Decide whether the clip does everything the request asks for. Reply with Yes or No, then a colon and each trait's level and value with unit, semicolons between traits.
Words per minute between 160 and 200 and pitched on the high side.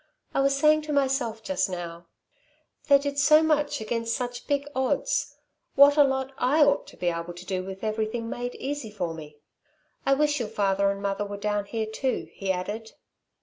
Yes: average, 190 wpm; high, 230 Hz